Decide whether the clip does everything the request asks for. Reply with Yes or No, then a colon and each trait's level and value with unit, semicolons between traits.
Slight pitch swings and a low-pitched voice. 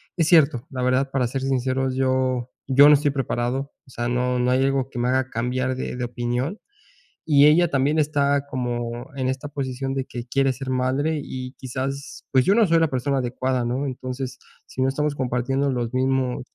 Yes: narrow, 1.8 semitones; low, 130 Hz